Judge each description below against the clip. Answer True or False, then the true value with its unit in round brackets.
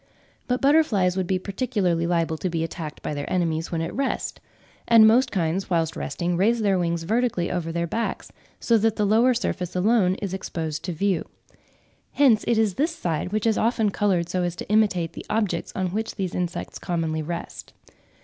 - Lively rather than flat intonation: False (4.4 semitones)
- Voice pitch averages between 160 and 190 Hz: True (185 Hz)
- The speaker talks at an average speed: True (190 wpm)